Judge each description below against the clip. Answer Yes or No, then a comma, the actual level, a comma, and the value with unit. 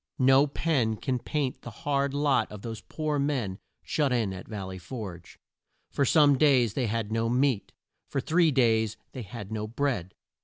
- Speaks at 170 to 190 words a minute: Yes, average, 180 wpm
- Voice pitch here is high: No, low, 125 Hz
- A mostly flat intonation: No, average, 4.6 semitones